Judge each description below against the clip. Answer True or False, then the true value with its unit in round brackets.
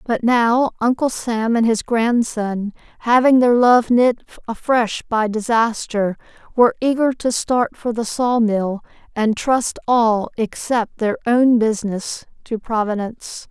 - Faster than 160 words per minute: False (140 wpm)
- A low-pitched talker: False (230 Hz)